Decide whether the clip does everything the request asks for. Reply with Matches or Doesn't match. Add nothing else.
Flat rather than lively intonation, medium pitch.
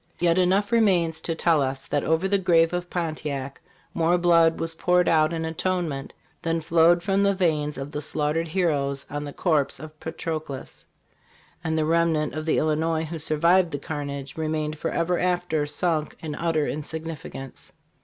Matches